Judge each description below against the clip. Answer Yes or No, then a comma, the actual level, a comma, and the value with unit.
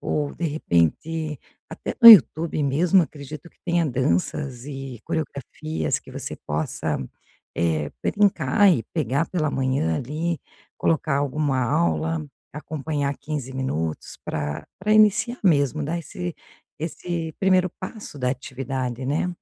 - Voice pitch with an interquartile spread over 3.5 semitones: Yes, average, 4.4 semitones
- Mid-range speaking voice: Yes, medium, 150 Hz